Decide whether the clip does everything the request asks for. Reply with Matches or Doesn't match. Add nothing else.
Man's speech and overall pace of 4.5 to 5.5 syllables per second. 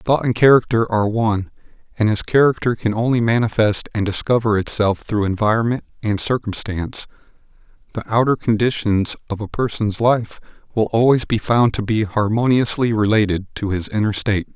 Matches